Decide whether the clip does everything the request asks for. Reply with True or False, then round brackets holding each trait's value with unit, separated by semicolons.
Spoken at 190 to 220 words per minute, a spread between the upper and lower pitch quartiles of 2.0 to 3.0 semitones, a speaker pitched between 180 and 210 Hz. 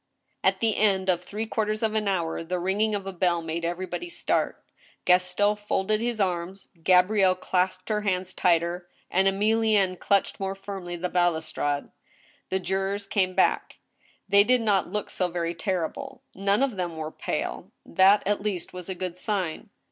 False (170 wpm; 2.6 semitones; 190 Hz)